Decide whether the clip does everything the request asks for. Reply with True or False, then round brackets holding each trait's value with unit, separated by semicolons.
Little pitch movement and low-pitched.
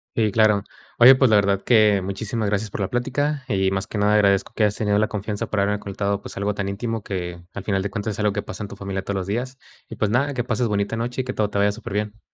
True (2.2 semitones; 105 Hz)